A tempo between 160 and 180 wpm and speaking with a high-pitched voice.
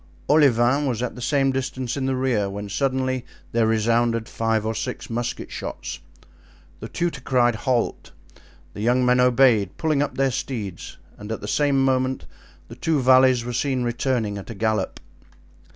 No: average, 170 wpm; low, 125 Hz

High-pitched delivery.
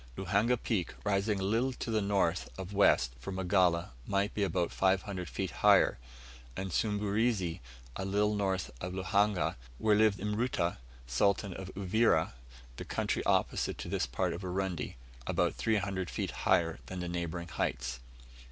No: very low, 95 Hz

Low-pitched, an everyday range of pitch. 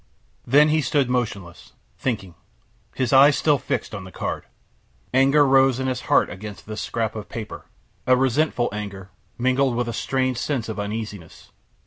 Yes: low, 125 Hz; average, 4.0 semitones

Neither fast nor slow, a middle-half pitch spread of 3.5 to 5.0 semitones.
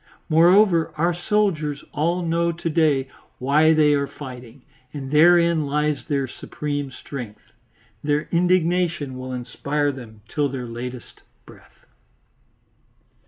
No: slow, 120 wpm; average, 3.9 semitones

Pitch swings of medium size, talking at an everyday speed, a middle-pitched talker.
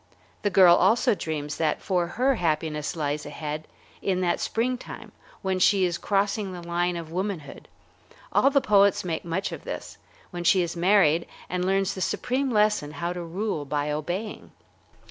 Yes: average, 3.6 semitones; average, 165 wpm; medium, 180 Hz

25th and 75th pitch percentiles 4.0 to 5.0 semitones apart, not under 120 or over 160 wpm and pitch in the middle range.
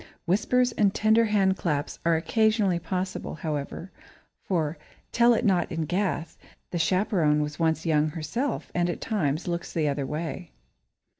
Yes: average, 4.6 semitones; average, 150 wpm; medium, 175 Hz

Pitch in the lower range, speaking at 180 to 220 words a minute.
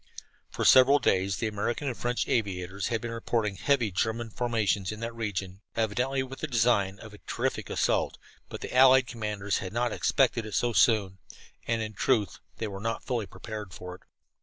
Yes: low, 110 Hz; average, 185 wpm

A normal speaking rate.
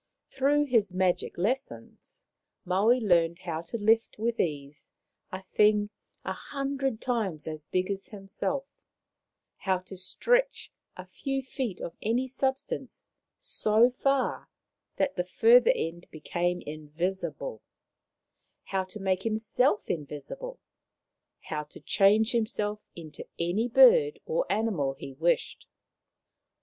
No: slow, 120 wpm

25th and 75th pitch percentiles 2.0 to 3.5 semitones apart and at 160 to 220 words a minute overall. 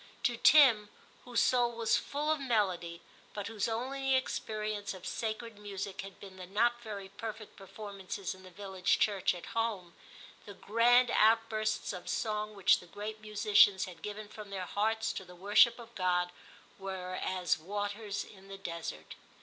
Yes: average, 2.9 semitones; average, 175 wpm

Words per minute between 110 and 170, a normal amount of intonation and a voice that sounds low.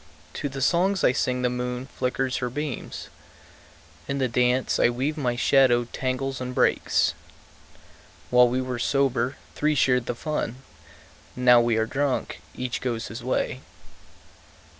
No: average, 145 wpm; narrow, 1.7 semitones; low, 125 Hz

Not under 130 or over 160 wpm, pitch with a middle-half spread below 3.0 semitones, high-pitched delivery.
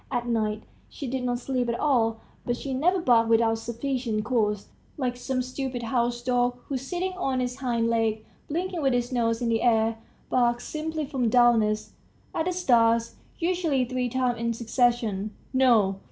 No: average, 170 wpm; narrow, 2.6 semitones; high, 245 Hz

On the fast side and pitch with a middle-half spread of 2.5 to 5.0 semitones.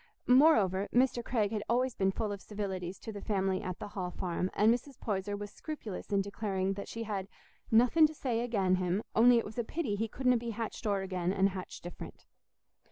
Yes: fast, 210 wpm; average, 3.6 semitones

